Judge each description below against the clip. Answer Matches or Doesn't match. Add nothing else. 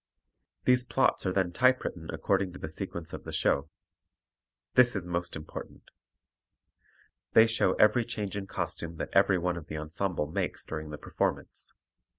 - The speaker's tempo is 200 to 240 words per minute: Doesn't match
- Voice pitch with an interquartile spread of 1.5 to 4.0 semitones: Doesn't match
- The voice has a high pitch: Doesn't match